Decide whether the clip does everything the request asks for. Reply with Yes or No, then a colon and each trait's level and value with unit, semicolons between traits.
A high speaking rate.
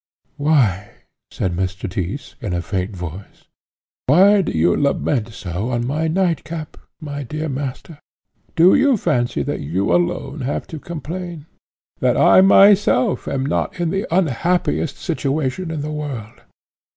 No: average, 140 wpm